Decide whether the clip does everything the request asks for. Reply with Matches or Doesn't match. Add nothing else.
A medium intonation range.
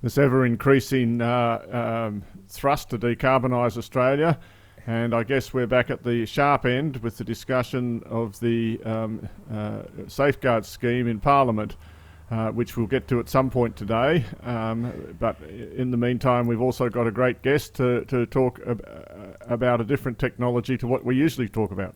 Doesn't match